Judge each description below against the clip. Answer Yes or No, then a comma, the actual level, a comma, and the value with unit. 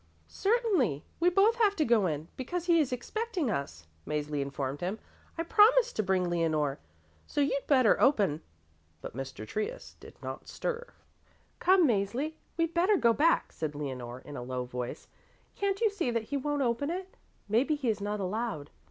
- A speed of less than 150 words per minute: No, average, 175 wpm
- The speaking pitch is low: No, high, 235 Hz